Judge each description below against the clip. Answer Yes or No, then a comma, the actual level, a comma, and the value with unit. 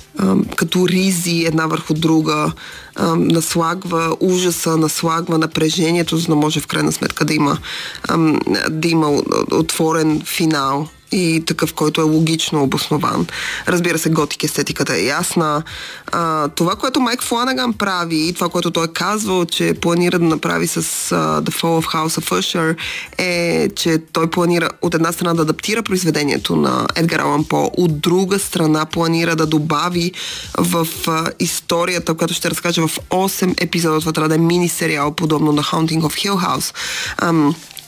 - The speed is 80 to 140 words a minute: No, average, 150 wpm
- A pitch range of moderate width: No, narrow, 1.9 semitones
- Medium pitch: Yes, medium, 165 Hz